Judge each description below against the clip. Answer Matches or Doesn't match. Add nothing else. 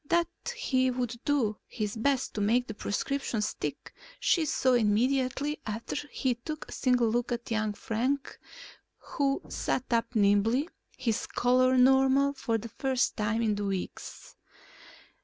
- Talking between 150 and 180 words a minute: Doesn't match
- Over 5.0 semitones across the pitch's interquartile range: Doesn't match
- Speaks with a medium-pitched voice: Doesn't match